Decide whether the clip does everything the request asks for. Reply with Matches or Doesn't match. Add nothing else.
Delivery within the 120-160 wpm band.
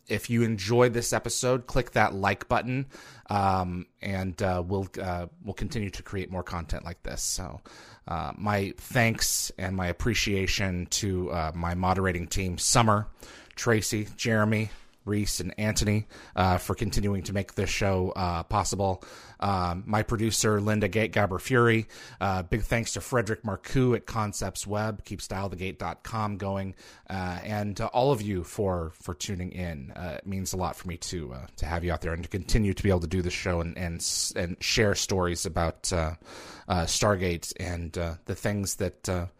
Doesn't match